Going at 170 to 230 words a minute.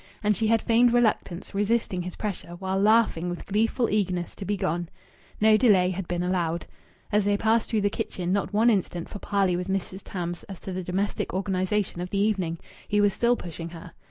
Yes: fast, 205 wpm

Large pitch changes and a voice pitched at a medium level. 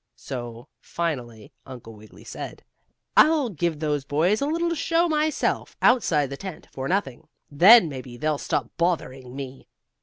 Yes: wide, 8.3 semitones; medium, 150 Hz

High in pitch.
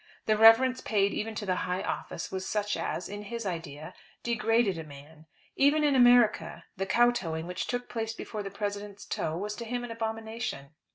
Yes: high, 210 Hz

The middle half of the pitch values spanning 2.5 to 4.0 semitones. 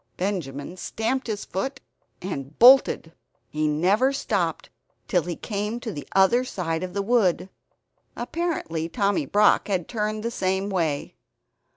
No: average, 5.0 semitones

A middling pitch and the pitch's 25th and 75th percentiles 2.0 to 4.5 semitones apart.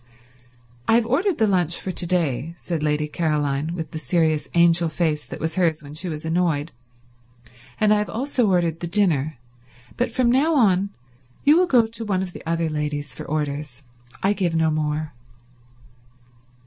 No: medium, 170 Hz; average, 4.9 semitones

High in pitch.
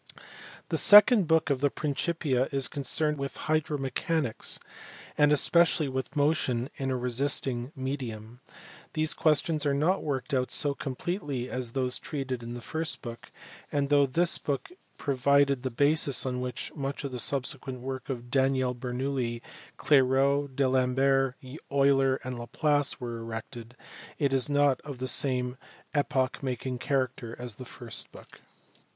No: low, 135 Hz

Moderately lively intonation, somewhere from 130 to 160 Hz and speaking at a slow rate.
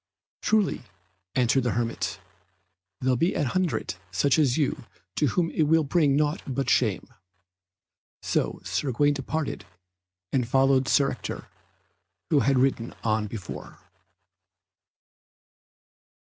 Yes: average, 3.7 semitones; low, 135 Hz; slow, 115 wpm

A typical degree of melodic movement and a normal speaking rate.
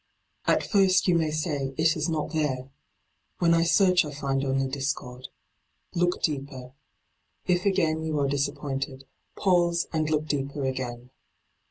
Yes: average, 3.7 semitones; average, 145 wpm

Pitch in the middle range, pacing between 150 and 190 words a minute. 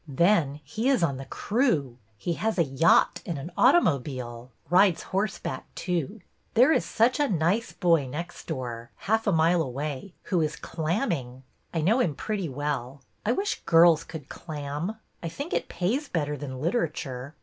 Yes: medium, 165 Hz; average, 170 wpm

